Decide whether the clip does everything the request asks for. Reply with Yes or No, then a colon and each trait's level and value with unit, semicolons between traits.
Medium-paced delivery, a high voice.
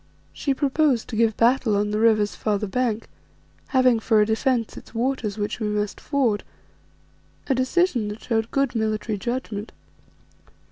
Yes: average, 150 wpm; high, 225 Hz